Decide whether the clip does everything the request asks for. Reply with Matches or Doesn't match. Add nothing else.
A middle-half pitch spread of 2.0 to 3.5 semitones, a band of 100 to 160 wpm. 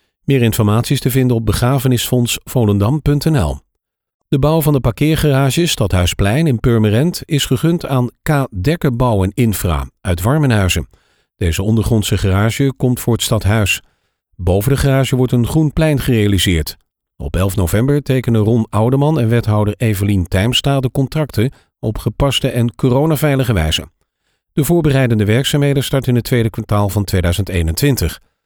Doesn't match